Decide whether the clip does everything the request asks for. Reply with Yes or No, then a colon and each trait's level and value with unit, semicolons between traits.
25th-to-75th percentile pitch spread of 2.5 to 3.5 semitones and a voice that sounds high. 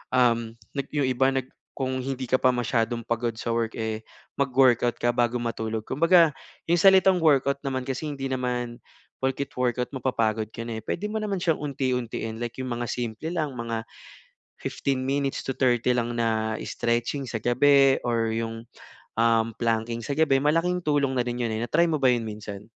No: average, 3.1 semitones; low, 125 Hz